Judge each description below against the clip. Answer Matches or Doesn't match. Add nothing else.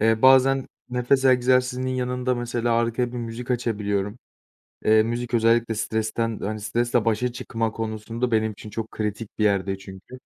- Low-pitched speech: Matches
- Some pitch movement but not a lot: Doesn't match